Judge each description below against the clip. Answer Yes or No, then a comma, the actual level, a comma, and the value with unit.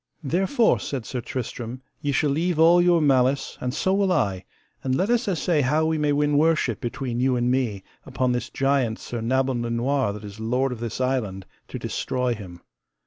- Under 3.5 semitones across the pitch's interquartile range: No, average, 4.1 semitones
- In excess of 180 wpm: Yes, average, 200 wpm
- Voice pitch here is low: Yes, low, 130 Hz